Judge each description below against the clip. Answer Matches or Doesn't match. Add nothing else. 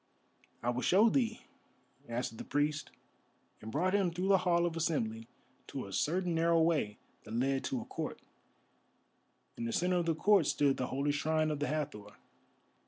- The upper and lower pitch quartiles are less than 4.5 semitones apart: Doesn't match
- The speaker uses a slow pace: Doesn't match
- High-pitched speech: Doesn't match